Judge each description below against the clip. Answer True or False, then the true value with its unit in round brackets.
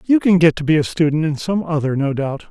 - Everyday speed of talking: False (290 wpm)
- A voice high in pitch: False (160 Hz)